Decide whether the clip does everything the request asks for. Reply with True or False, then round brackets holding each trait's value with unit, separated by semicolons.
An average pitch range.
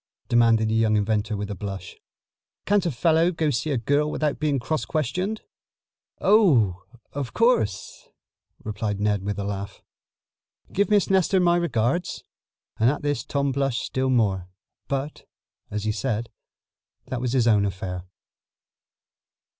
False (6.7 semitones)